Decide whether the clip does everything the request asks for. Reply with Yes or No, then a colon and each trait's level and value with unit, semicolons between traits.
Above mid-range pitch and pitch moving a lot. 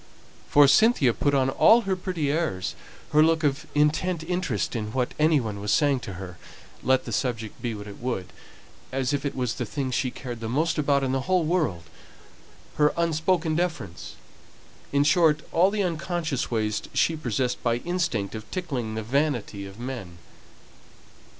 No: medium, 140 Hz; wide, 5.7 semitones